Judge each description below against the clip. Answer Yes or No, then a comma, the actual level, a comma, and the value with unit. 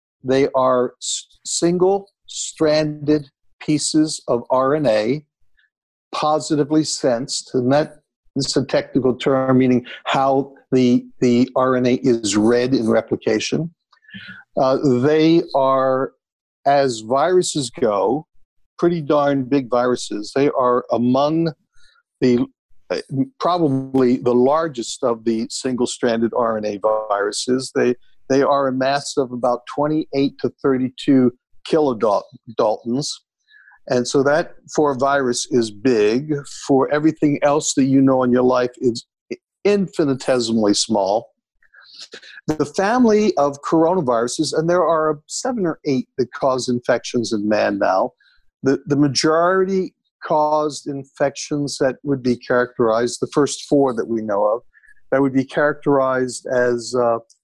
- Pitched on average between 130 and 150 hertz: Yes, low, 135 Hz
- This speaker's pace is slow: Yes, slow, 120 wpm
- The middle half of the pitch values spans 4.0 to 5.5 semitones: No, average, 3.3 semitones